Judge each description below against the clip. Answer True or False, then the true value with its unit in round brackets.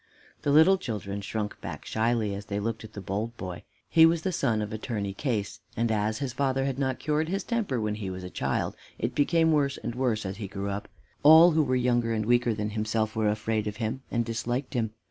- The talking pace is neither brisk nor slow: False (230 wpm)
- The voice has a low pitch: True (115 Hz)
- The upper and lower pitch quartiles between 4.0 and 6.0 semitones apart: True (4.3 semitones)